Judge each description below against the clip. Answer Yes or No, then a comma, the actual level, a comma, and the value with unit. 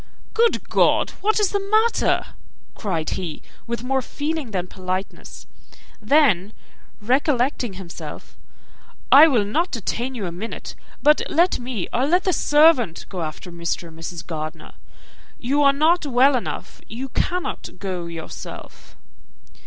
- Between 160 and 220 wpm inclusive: No, slow, 135 wpm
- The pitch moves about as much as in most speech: No, wide, 8.4 semitones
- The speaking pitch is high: Yes, high, 245 Hz